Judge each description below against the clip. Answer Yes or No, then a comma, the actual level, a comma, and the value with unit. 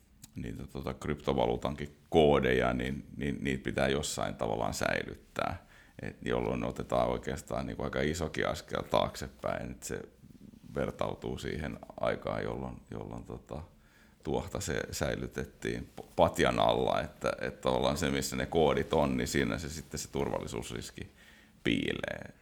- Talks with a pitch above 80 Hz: No, very low, 65 Hz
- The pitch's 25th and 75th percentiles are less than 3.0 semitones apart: Yes, narrow, 2.4 semitones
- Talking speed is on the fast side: No, average, 135 wpm